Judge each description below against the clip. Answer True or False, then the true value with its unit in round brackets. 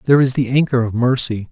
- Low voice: True (125 Hz)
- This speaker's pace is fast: True (235 wpm)